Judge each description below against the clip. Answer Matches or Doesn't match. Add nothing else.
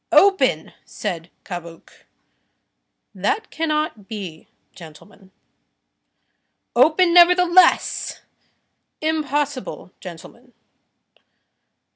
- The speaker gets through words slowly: Matches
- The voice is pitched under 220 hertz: Doesn't match